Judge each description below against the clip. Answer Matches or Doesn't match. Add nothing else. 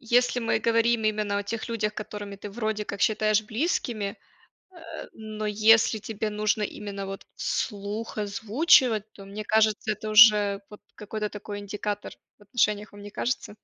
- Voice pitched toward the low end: Doesn't match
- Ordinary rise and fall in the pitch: Doesn't match